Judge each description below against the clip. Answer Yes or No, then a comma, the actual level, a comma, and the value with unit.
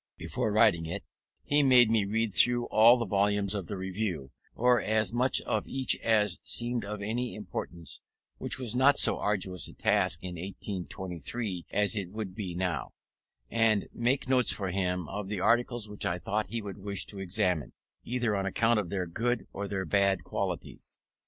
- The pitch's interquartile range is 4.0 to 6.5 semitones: No, average, 3.6 semitones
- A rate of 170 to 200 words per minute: Yes, average, 180 wpm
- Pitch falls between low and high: No, low, 105 Hz